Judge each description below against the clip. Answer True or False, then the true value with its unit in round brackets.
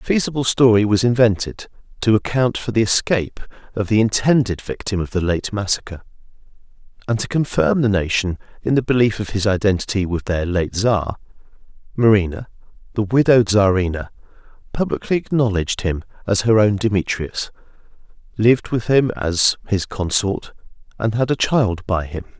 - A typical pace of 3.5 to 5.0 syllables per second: False (5.3 syllables/s)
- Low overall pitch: True (105 Hz)